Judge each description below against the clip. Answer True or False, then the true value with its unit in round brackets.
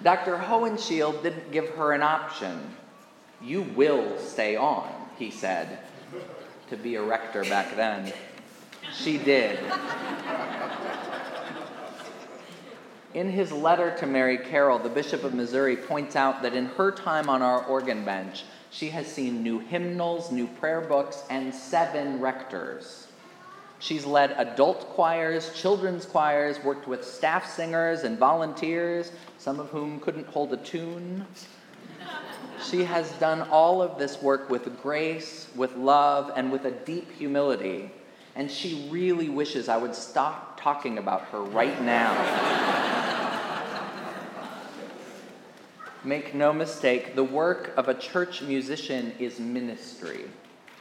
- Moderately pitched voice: True (150 Hz)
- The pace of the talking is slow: True (130 wpm)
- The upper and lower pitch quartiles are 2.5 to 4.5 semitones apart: True (4.2 semitones)